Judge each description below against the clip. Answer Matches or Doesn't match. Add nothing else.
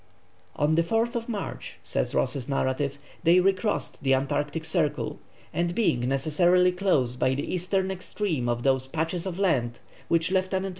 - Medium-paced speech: Matches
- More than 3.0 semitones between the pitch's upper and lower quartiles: Matches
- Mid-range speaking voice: Matches